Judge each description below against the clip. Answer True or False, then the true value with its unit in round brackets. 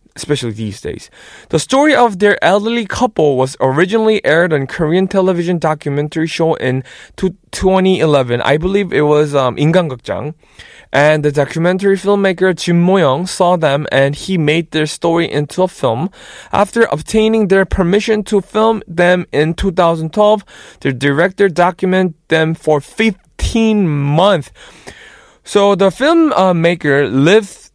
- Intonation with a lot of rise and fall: False (5.0 semitones)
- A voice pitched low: False (175 Hz)